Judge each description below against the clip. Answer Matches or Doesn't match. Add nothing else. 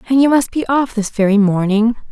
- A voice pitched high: Matches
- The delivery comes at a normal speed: Doesn't match